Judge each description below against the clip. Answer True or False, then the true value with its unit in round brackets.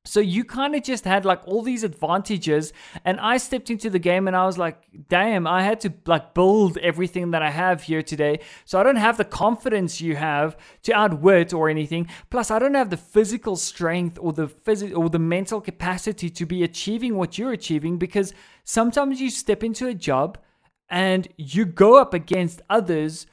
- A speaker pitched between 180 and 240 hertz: True (185 Hz)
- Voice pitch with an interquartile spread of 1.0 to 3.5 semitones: False (4.4 semitones)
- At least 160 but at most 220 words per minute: True (200 wpm)